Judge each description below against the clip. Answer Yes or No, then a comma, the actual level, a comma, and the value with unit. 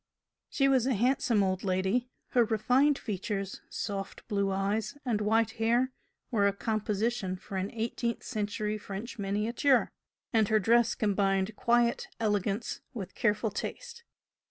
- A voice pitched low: No, high, 215 Hz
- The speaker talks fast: No, slow, 135 wpm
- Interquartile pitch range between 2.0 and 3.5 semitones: Yes, average, 3.0 semitones